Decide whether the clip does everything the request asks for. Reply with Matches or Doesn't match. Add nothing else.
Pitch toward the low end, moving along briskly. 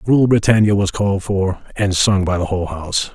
Matches